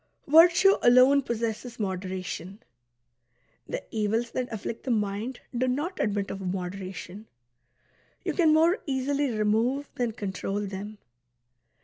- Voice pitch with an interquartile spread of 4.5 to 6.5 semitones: Yes, average, 4.9 semitones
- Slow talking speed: Yes, slow, 115 wpm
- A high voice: Yes, high, 225 Hz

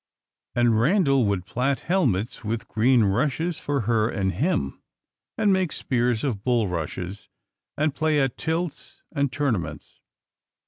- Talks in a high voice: No, low, 125 Hz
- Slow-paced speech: Yes, slow, 130 wpm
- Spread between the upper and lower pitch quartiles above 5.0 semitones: Yes, wide, 5.6 semitones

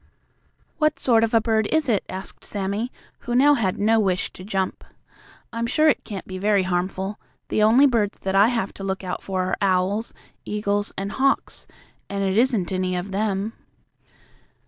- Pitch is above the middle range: Yes, high, 205 Hz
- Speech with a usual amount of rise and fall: Yes, average, 3.1 semitones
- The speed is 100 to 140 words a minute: No, average, 180 wpm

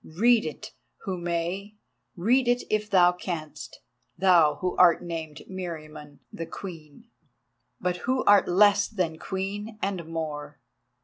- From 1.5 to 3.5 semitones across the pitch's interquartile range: No, average, 4.1 semitones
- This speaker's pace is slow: Yes, slow, 125 wpm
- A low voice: No, medium, 180 Hz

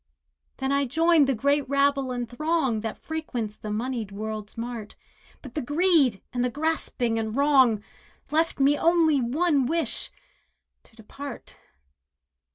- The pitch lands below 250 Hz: No, very high, 265 Hz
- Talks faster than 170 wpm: No, slow, 135 wpm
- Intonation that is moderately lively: Yes, average, 4.6 semitones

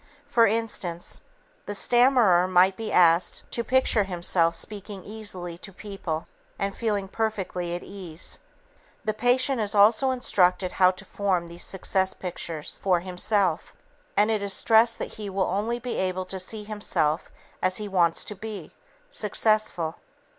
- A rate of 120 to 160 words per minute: Yes, average, 150 wpm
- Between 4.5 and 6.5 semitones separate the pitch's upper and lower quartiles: No, average, 3.2 semitones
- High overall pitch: Yes, high, 195 Hz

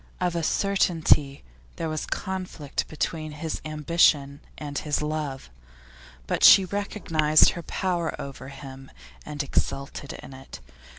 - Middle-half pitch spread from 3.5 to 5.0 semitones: No, average, 3.1 semitones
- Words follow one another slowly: Yes, slow, 125 wpm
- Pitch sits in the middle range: Yes, medium, 155 Hz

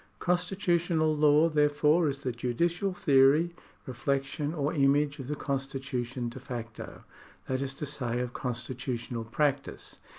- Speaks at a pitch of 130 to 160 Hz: Yes, medium, 140 Hz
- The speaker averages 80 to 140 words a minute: Yes, slow, 135 wpm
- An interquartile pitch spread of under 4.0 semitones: Yes, average, 3.0 semitones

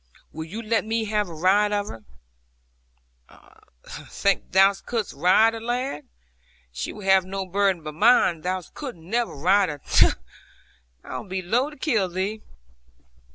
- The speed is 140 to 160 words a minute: Yes, average, 155 wpm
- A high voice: Yes, high, 195 Hz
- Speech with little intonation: No, average, 3.5 semitones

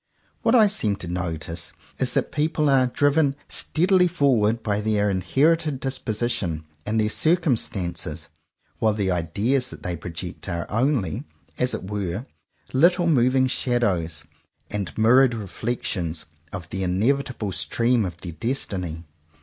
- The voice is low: Yes, low, 110 Hz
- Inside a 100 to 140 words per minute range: Yes, slow, 135 wpm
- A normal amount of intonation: No, wide, 6.7 semitones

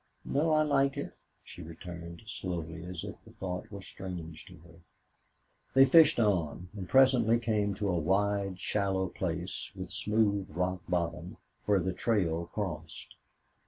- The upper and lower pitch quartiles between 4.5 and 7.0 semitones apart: No, average, 3.7 semitones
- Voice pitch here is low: Yes, very low, 95 Hz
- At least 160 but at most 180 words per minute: No, average, 150 wpm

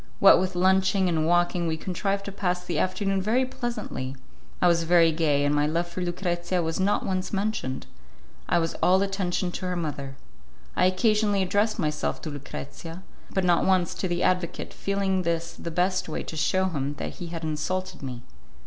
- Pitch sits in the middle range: Yes, medium, 180 Hz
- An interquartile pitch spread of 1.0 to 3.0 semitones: Yes, narrow, 2.6 semitones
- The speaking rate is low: No, average, 185 wpm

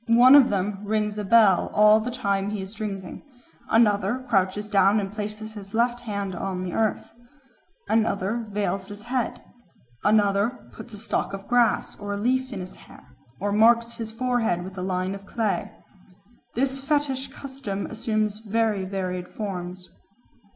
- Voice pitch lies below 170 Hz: No, high, 210 Hz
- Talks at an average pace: Yes, average, 160 wpm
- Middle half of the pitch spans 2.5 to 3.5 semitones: Yes, average, 2.8 semitones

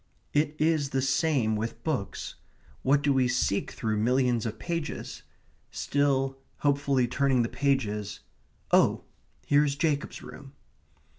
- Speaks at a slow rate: Yes, slow, 130 wpm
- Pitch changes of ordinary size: Yes, average, 3.0 semitones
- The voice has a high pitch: No, low, 135 Hz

